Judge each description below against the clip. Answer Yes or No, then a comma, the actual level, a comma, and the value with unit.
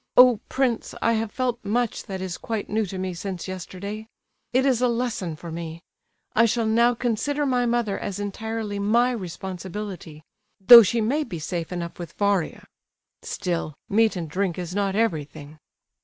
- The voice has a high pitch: Yes, high, 205 Hz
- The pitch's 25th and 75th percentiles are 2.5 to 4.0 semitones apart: No, average, 4.5 semitones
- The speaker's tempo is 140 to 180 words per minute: Yes, average, 170 wpm